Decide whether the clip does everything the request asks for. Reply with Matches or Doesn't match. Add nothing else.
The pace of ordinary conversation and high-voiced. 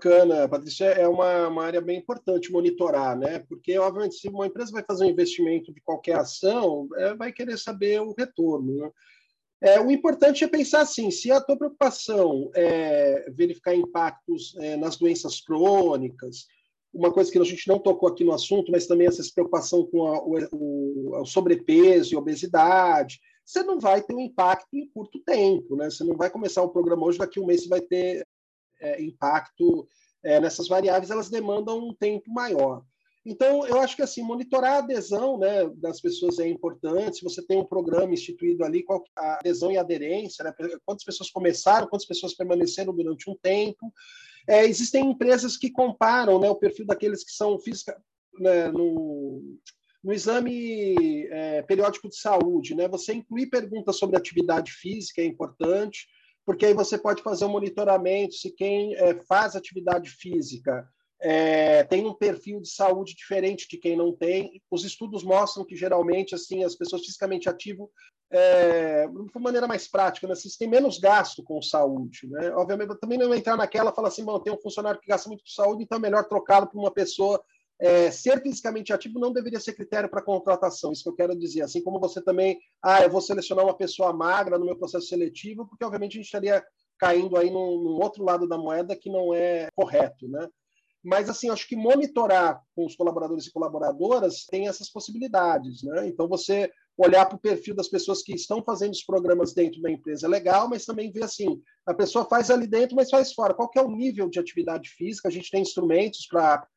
Doesn't match